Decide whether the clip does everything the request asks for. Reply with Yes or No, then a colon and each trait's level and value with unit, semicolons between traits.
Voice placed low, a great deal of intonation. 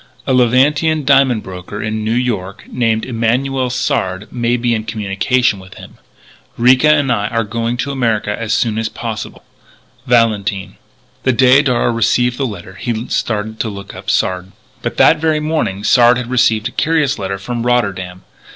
No: low, 115 Hz; average, 3.3 semitones